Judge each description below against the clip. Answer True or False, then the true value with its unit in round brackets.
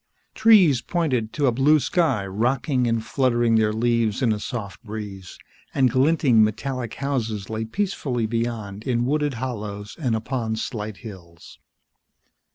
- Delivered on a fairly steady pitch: False (3.6 semitones)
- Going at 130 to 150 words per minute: True (140 wpm)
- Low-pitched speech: True (115 Hz)